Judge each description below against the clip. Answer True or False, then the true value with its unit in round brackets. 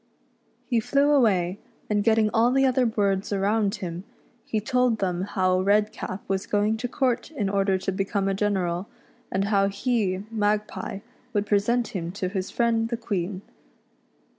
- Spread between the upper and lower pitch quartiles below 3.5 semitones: True (2.8 semitones)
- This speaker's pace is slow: False (160 wpm)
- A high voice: True (205 Hz)